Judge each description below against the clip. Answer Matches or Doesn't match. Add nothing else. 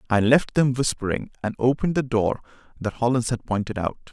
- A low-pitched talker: Matches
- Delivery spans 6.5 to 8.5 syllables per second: Doesn't match